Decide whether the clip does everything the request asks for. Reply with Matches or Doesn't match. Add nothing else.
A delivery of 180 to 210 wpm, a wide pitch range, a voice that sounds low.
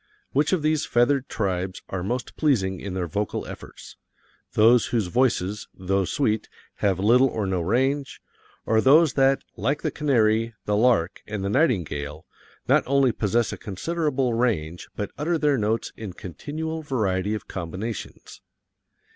Doesn't match